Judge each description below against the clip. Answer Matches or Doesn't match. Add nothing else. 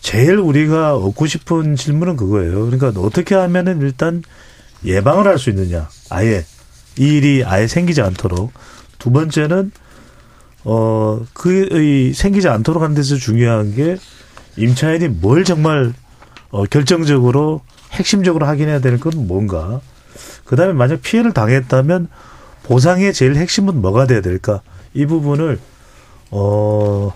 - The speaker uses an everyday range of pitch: Doesn't match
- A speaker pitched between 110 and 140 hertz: Matches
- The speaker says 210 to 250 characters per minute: Doesn't match